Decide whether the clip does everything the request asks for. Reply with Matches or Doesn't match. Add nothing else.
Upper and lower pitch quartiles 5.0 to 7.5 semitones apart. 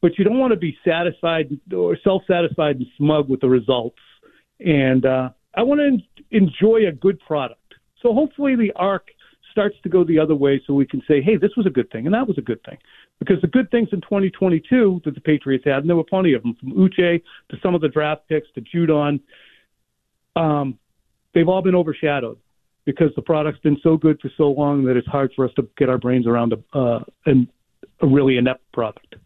Matches